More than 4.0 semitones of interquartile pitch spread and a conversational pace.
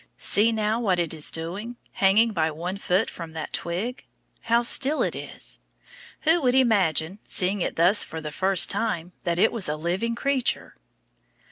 Yes: average, 5.3 semitones; average, 170 wpm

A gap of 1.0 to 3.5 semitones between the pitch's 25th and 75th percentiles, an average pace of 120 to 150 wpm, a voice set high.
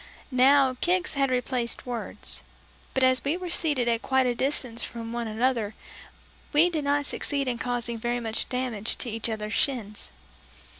No: average, 3.1 semitones; average, 165 wpm; very high, 250 Hz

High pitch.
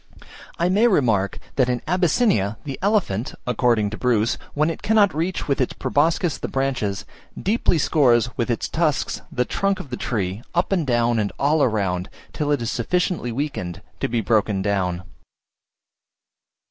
No: low, 125 Hz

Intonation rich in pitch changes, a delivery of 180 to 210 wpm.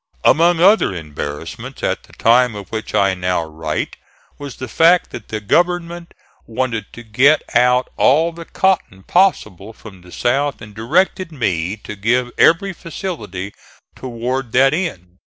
No: wide, 8.6 semitones; average, 150 wpm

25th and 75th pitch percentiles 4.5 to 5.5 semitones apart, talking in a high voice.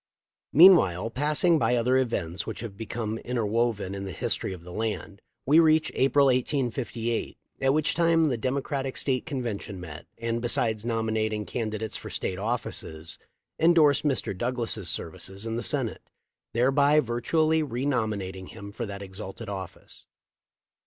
No: average, 5.0 semitones; low, 115 Hz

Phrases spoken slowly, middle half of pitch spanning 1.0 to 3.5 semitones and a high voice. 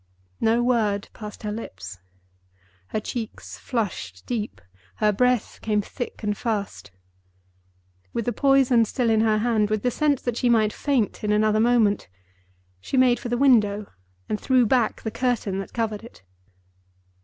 No: average, 155 wpm; average, 2.7 semitones; high, 225 Hz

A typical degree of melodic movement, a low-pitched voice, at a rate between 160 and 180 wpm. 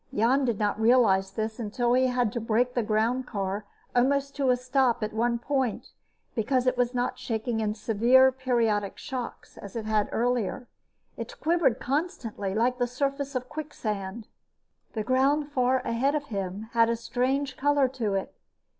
No: average, 3.1 semitones; high, 245 Hz; average, 165 wpm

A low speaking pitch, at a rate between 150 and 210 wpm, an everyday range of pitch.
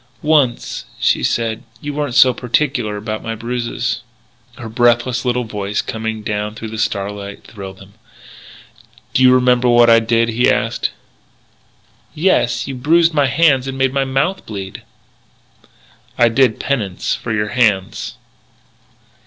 No: low, 120 Hz; average, 140 wpm; average, 3.4 semitones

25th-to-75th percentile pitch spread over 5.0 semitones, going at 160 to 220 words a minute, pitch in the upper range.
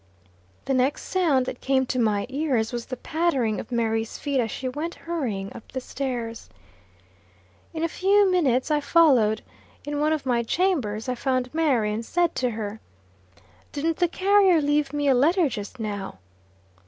Yes: wide, 5.5 semitones; average, 170 wpm; very high, 265 Hz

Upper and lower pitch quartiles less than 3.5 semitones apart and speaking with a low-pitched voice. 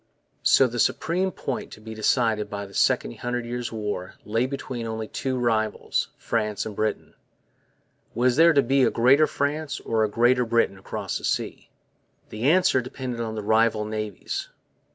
Yes: average, 3.0 semitones; low, 115 Hz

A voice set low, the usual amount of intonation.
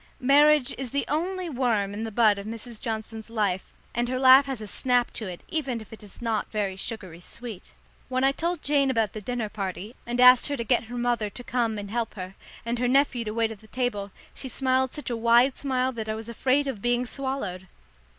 No: high, 240 Hz; average, 3.3 semitones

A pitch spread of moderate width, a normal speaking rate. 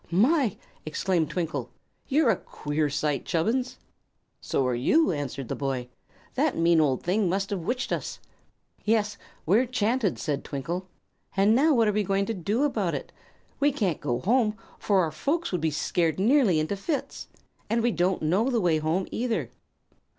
No: wide, 6.7 semitones; average, 170 wpm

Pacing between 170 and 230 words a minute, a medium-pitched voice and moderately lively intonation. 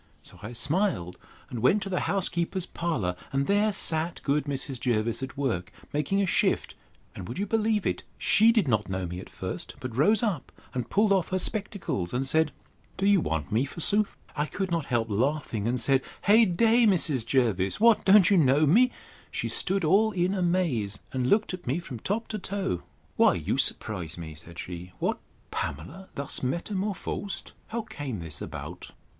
No: average, 185 wpm; medium, 155 Hz; wide, 8.9 semitones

